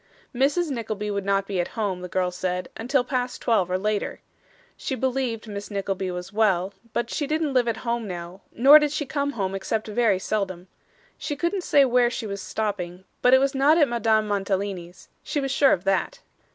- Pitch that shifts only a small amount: No, average, 5.3 semitones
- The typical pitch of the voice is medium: No, high, 220 Hz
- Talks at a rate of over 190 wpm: Yes, average, 200 wpm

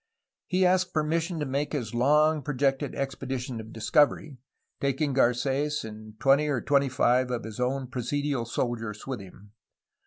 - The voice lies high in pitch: No, low, 135 Hz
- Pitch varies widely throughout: No, average, 3.5 semitones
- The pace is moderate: Yes, average, 150 wpm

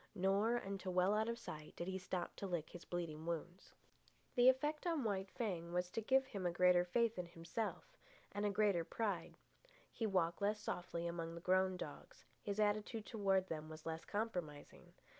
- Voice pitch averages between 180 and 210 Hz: Yes, high, 190 Hz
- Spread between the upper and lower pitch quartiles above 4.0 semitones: No, average, 3.7 semitones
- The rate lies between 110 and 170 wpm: No, average, 185 wpm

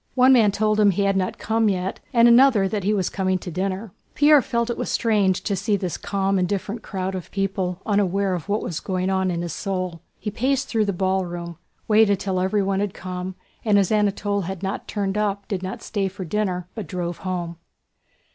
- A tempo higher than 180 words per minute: Yes, fast, 205 wpm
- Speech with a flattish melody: Yes, narrow, 2.2 semitones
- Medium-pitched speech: No, high, 195 Hz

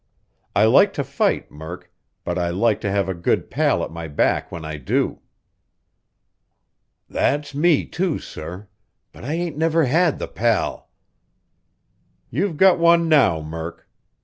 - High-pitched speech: No, low, 120 Hz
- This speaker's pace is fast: No, average, 150 wpm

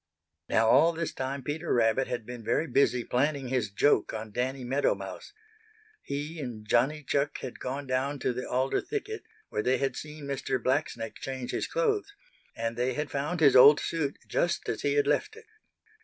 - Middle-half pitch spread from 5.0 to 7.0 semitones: No, average, 3.3 semitones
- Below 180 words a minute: No, average, 185 wpm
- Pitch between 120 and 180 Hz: Yes, low, 135 Hz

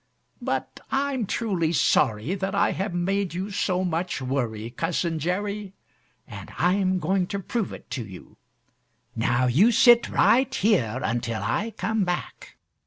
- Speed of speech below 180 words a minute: Yes, average, 145 wpm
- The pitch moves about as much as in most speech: No, wide, 6.9 semitones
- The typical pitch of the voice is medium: Yes, medium, 180 Hz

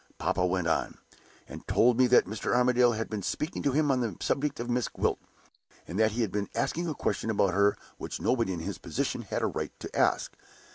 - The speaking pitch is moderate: No, low, 115 Hz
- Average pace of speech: No, fast, 225 wpm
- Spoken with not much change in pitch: No, average, 3.8 semitones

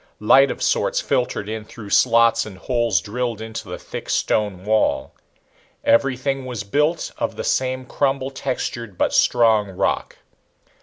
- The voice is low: Yes, low, 115 Hz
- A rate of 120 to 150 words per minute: Yes, average, 145 wpm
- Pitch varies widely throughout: No, average, 3.7 semitones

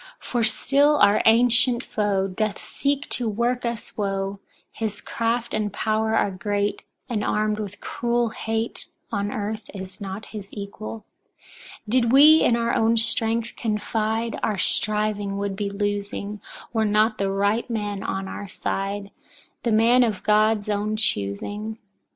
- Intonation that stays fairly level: Yes, narrow, 2.1 semitones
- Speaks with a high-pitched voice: Yes, high, 215 Hz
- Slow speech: No, average, 150 wpm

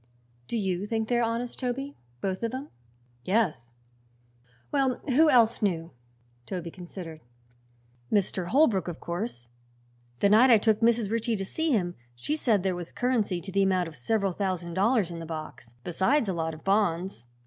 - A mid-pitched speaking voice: No, high, 195 Hz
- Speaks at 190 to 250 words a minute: No, average, 170 wpm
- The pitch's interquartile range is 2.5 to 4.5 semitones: No, average, 5.0 semitones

